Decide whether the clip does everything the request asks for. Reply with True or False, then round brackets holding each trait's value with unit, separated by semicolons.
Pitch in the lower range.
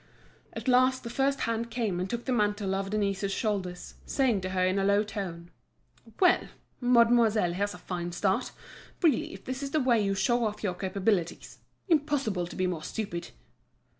False (210 Hz)